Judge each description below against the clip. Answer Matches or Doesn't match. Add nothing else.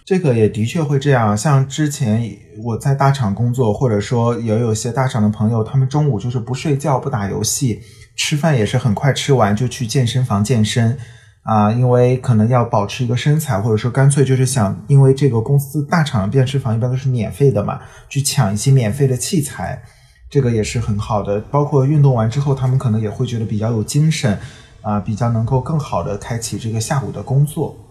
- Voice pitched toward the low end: Matches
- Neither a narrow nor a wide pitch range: Matches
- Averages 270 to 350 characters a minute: Matches